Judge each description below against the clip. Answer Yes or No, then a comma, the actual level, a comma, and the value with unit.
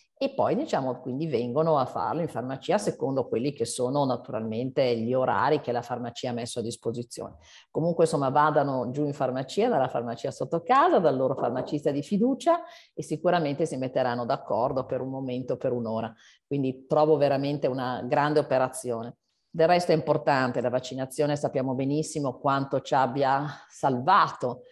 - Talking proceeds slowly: No, average, 160 wpm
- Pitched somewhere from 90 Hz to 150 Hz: Yes, low, 135 Hz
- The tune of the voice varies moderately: Yes, average, 3.4 semitones